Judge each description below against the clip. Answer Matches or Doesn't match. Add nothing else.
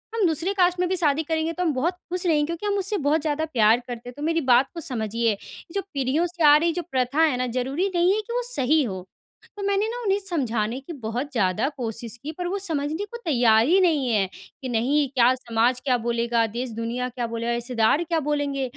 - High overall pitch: Matches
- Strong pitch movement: Matches